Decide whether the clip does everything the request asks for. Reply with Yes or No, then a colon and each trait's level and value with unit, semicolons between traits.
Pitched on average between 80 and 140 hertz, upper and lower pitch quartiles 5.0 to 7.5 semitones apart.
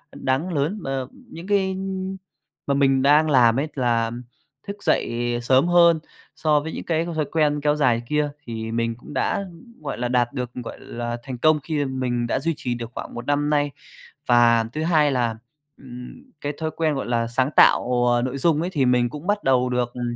No: low, 135 Hz; average, 4.4 semitones